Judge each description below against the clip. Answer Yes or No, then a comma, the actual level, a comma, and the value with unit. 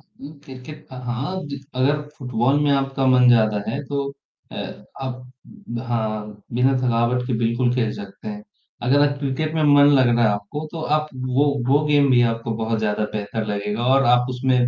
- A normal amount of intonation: Yes, average, 3.6 semitones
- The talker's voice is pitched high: No, low, 125 Hz